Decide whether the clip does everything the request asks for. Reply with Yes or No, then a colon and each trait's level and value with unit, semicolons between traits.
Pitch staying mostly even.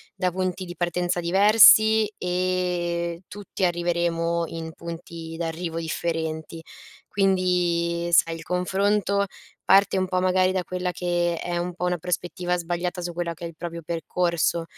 Yes: narrow, 1.3 semitones